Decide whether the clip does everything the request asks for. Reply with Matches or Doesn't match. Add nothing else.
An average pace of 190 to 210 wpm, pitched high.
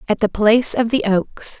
Doesn't match